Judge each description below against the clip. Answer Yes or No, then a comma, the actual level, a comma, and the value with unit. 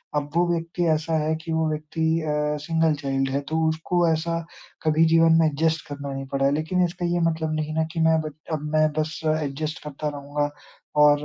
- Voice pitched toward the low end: No, medium, 155 Hz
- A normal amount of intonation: No, narrow, 1.7 semitones